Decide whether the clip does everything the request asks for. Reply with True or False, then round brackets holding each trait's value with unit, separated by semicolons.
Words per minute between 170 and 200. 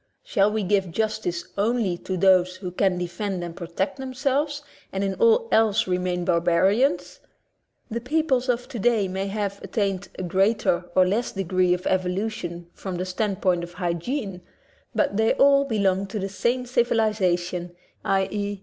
False (160 wpm)